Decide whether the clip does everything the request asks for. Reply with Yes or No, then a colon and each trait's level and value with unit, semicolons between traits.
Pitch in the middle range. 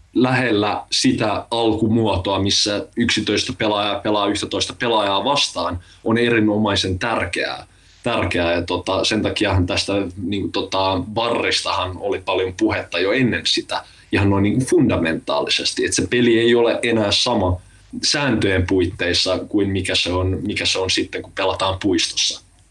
No: low, 100 Hz